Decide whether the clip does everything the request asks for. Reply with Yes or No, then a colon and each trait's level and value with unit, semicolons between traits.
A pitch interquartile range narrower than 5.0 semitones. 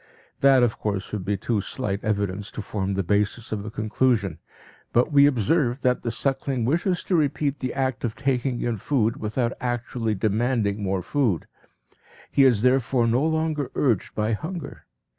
Yes: average, 4.2 semitones